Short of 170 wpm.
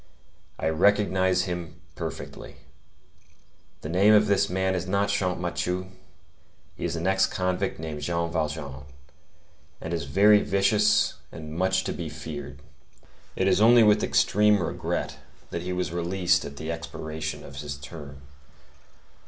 Yes: average, 140 wpm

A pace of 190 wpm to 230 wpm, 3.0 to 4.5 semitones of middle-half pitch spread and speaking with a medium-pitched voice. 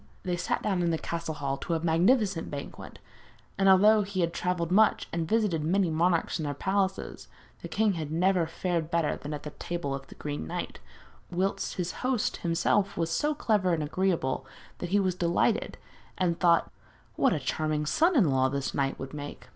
Yes: average, 195 wpm; average, 3.7 semitones; medium, 170 Hz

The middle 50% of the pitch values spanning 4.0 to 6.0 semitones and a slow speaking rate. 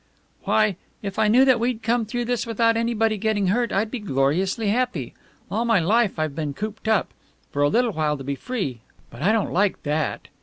No: average, 5.2 semitones; fast, 205 wpm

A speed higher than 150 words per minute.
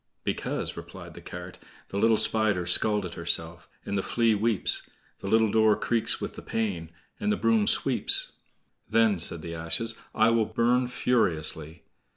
Yes: average, 160 wpm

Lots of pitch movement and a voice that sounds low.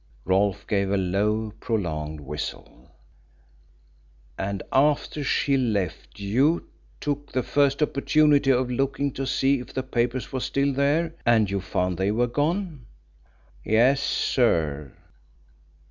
Yes: wide, 5.9 semitones; low, 125 Hz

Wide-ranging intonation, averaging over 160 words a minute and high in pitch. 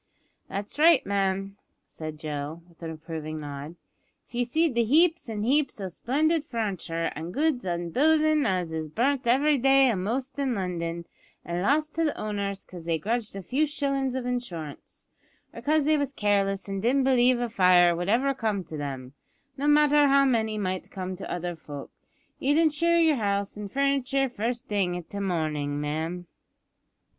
Yes: wide, 7.8 semitones; average, 175 wpm; high, 210 Hz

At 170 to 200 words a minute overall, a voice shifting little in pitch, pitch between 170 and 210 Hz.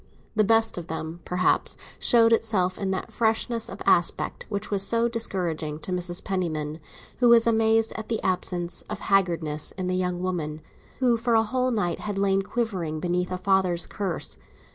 No: average, 175 wpm; average, 4.3 semitones; high, 190 Hz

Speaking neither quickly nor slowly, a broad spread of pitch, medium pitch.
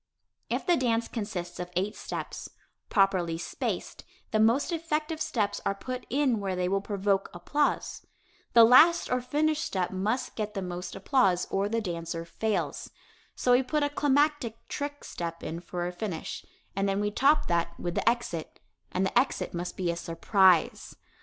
No: average, 170 wpm; wide, 6.2 semitones; high, 205 Hz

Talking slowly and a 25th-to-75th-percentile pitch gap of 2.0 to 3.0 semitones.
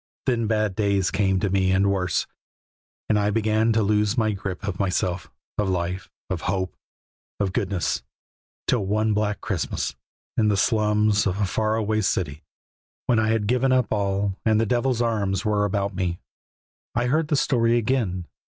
No: average, 170 wpm; narrow, 2.5 semitones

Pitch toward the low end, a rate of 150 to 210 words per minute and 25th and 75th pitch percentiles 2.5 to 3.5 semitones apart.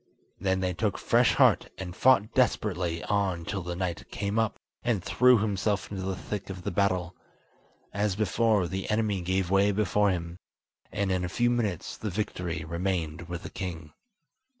Yes: very low, 95 Hz; average, 175 wpm; average, 2.8 semitones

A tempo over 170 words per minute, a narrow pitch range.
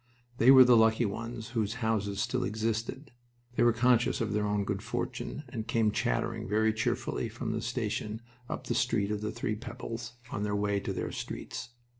Yes: average, 190 wpm; narrow, 2.2 semitones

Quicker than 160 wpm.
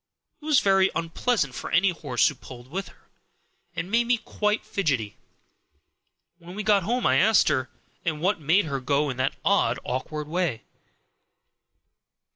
No: average, 155 wpm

